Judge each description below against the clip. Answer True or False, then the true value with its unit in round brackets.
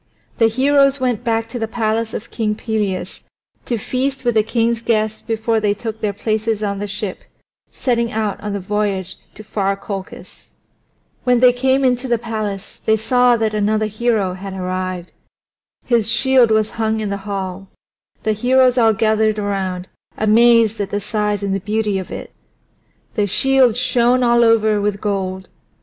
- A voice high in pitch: True (220 Hz)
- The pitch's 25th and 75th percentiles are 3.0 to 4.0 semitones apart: False (2.6 semitones)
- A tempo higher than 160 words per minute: True (170 wpm)